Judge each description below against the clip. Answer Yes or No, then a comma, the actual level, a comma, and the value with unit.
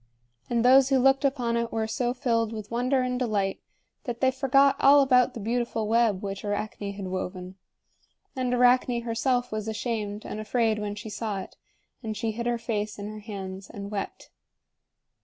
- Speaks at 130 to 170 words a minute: No, average, 180 wpm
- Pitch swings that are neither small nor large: Yes, average, 3.0 semitones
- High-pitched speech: Yes, high, 230 Hz